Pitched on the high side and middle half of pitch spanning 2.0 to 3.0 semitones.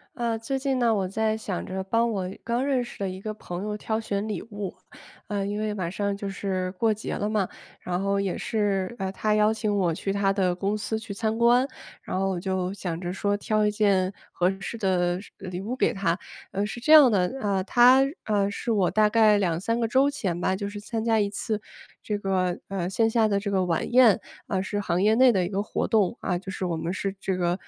Yes: high, 205 Hz; average, 2.7 semitones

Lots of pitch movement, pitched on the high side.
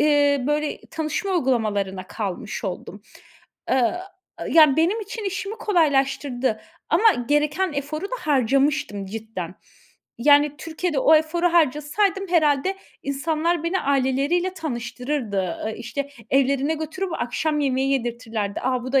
No: average, 4.6 semitones; very high, 285 Hz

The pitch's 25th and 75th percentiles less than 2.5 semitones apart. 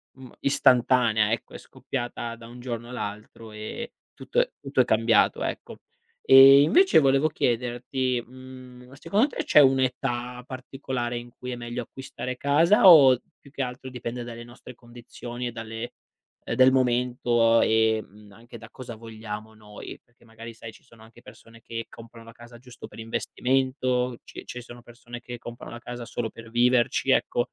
Yes: narrow, 1.9 semitones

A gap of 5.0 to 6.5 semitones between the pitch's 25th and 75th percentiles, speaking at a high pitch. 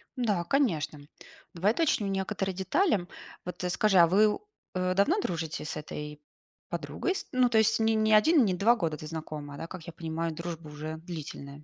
No: average, 5.3 semitones; medium, 180 Hz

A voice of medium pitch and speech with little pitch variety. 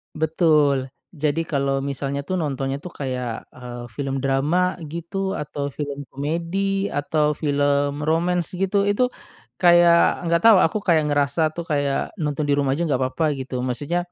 No: medium, 145 Hz; average, 3.4 semitones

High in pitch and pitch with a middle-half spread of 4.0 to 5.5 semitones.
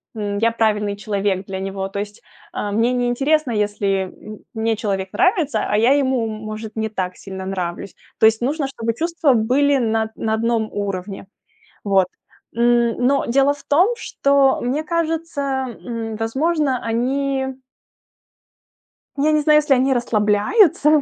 Yes: high, 230 Hz; average, 5.0 semitones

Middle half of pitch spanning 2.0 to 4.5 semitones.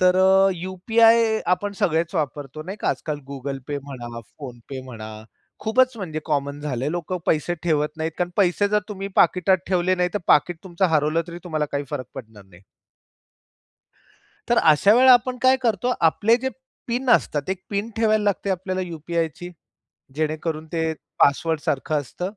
No: average, 5.1 semitones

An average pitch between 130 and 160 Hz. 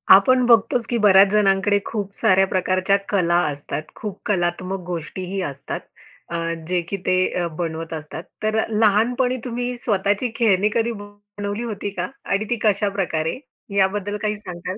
No: high, 200 Hz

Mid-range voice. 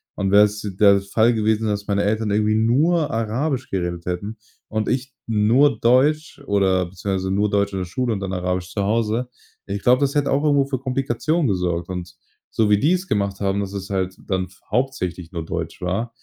No: low, 105 Hz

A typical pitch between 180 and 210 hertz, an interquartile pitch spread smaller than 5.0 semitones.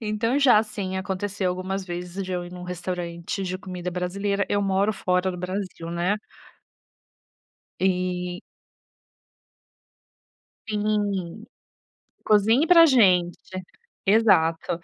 Yes: high, 190 Hz; narrow, 2.4 semitones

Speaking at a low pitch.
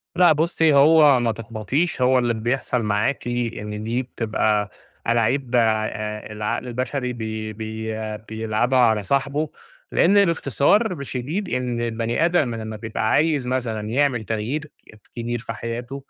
Yes: low, 120 Hz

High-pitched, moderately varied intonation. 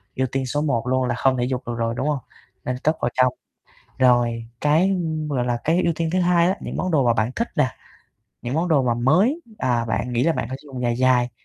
No: low, 130 Hz; average, 4.5 semitones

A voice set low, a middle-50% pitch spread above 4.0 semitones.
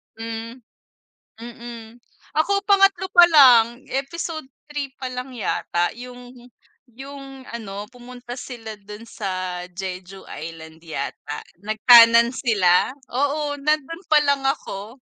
No: high, 240 Hz; average, 4.7 semitones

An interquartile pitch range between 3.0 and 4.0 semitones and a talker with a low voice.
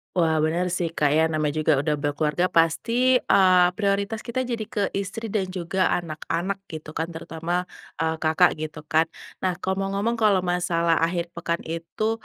No: average, 3.5 semitones; medium, 175 Hz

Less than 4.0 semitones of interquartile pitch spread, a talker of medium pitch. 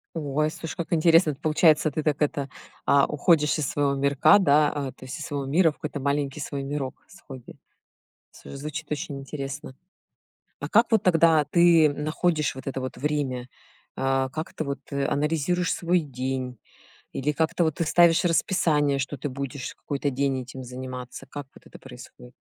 Yes: average, 2.7 semitones; medium, 145 Hz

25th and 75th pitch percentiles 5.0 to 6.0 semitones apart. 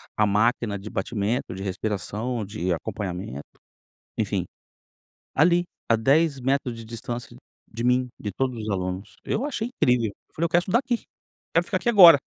Yes: wide, 5.5 semitones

